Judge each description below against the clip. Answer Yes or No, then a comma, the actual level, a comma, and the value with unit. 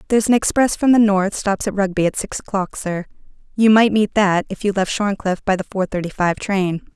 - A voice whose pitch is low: No, high, 200 Hz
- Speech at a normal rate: No, fast, 235 wpm